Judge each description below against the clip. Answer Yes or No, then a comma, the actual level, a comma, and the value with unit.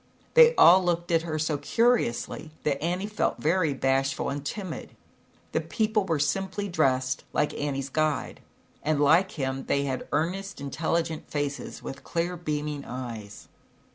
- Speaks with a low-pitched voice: No, medium, 155 Hz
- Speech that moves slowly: No, average, 145 wpm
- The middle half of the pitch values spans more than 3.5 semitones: Yes, average, 4.2 semitones